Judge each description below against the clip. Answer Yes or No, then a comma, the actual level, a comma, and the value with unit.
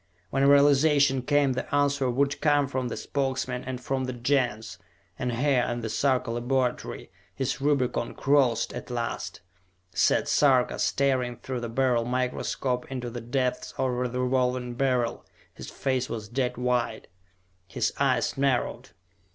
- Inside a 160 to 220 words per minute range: No, average, 145 wpm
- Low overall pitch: Yes, low, 130 Hz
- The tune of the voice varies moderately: No, narrow, 1.9 semitones